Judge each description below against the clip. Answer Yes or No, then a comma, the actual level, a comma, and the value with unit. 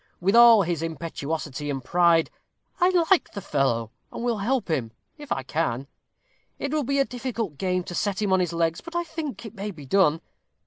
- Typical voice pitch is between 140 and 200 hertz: Yes, medium, 185 Hz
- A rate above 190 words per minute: Yes, average, 200 wpm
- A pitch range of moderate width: No, wide, 7.2 semitones